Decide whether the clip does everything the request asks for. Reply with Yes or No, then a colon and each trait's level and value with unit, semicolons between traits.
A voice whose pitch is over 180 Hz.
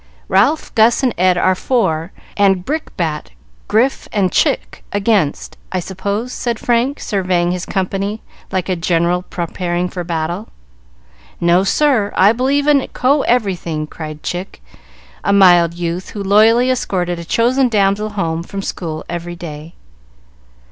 Yes: high, 190 Hz